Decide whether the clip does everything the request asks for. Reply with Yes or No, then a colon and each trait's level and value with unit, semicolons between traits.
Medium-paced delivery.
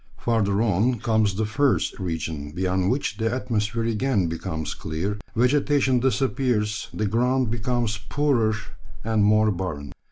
No: slow, 130 wpm